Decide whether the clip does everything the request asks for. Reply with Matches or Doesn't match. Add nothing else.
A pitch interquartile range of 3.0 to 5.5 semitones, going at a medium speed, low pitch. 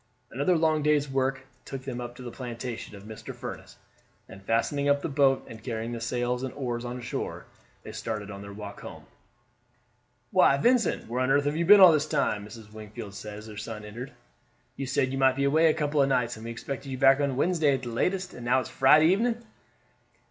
Doesn't match